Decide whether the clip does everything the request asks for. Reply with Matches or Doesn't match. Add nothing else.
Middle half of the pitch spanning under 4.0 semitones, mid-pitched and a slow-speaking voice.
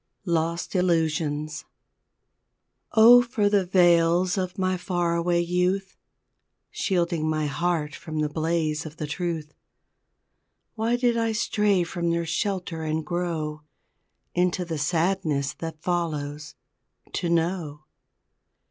Matches